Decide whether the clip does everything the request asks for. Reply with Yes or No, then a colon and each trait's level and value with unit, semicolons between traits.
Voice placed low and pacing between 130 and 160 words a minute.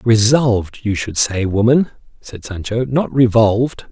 Yes: low, 115 Hz; average, 140 wpm